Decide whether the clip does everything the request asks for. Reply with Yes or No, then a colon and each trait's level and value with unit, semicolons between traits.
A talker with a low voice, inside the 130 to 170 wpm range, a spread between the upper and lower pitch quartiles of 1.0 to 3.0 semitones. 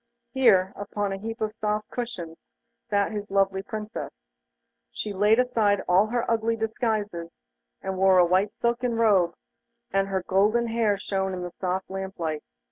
No: high, 205 Hz; average, 165 wpm; average, 2.7 semitones